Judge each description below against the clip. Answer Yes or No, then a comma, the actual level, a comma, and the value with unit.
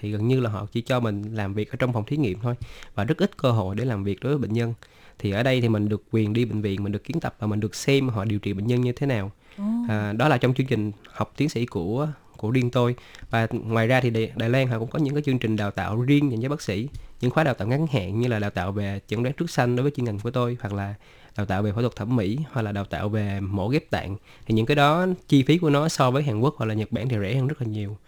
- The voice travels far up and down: No, average, 4.0 semitones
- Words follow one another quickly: Yes, fast, 315 wpm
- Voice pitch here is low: Yes, low, 115 Hz